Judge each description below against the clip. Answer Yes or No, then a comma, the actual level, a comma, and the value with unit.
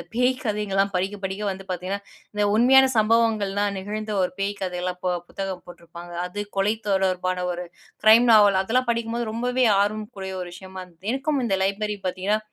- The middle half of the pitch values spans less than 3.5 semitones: Yes, narrow, 2.6 semitones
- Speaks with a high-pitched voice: Yes, high, 200 Hz